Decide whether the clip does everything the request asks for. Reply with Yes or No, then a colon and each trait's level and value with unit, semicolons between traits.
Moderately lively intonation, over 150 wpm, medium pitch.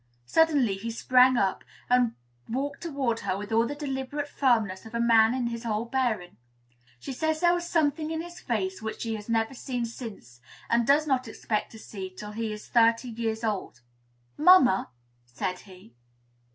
No: average, 3.9 semitones; average, 180 wpm; high, 235 Hz